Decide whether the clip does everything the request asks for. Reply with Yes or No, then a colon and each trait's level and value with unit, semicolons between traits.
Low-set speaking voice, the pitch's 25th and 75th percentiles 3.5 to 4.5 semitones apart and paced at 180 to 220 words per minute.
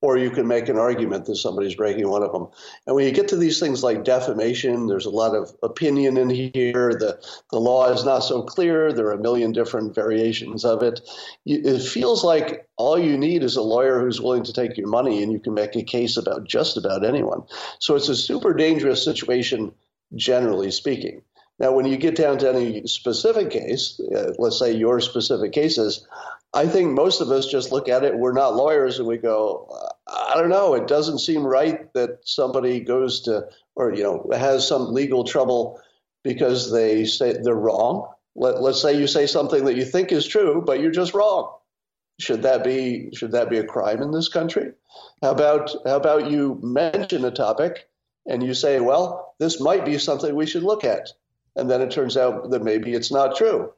Yes: low, 130 Hz; average, 4.0 semitones; fast, 205 wpm